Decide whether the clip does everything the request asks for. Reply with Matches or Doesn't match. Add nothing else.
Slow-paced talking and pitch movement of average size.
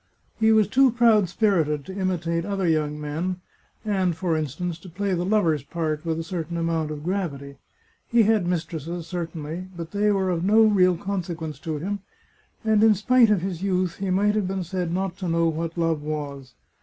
Doesn't match